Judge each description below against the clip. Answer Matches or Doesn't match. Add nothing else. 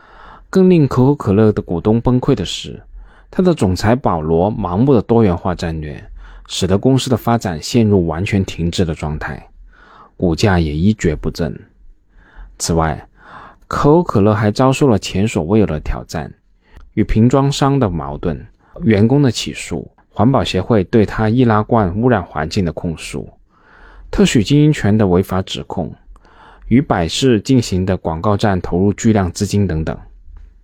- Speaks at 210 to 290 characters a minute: Matches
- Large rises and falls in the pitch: Matches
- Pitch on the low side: Matches